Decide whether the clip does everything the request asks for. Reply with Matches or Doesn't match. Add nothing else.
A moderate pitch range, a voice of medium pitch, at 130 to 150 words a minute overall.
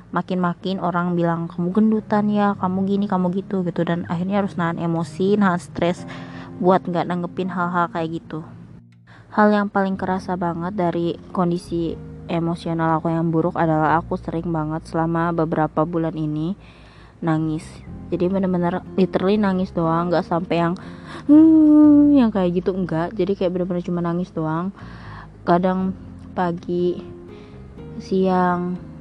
Doesn't match